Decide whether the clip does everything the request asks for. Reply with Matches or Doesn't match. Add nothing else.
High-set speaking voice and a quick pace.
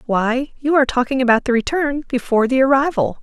Doesn't match